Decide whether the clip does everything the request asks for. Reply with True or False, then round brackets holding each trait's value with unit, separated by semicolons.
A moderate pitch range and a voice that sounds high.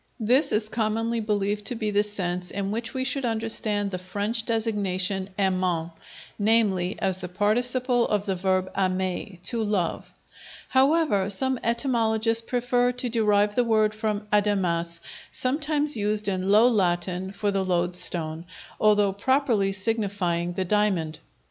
True (3.4 semitones; 205 Hz)